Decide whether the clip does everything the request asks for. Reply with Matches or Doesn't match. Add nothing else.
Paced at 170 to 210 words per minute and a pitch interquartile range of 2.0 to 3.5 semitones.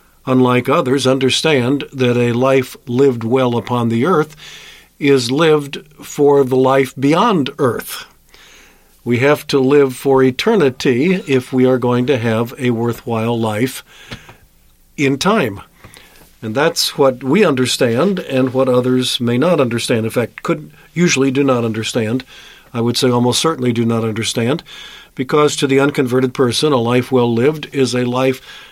Doesn't match